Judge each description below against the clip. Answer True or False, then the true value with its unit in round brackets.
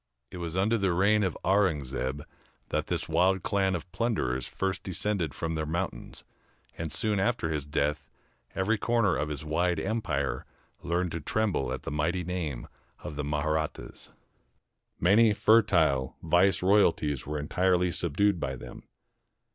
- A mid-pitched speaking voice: False (85 Hz)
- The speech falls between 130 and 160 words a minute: True (145 wpm)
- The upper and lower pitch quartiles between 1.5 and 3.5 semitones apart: False (4.6 semitones)